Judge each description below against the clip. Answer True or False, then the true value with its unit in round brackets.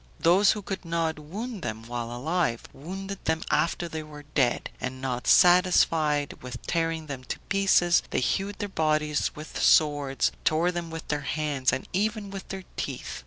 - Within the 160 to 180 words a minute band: True (170 wpm)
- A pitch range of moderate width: True (4.1 semitones)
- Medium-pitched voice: True (160 Hz)